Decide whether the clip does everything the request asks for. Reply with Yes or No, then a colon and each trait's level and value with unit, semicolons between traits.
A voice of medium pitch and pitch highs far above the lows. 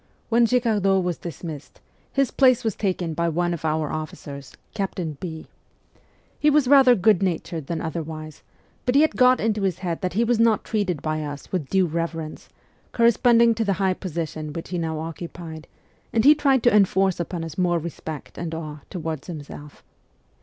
Yes: medium, 175 Hz; wide, 5.7 semitones